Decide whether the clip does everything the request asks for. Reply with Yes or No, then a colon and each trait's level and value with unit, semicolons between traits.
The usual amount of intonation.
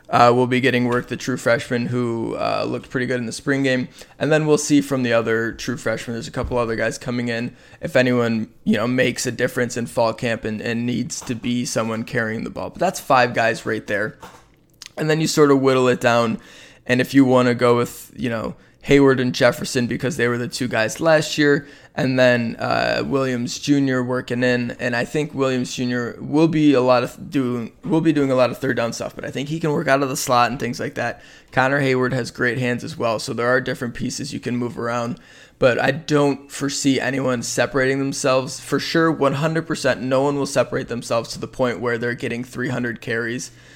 No: narrow, 2.2 semitones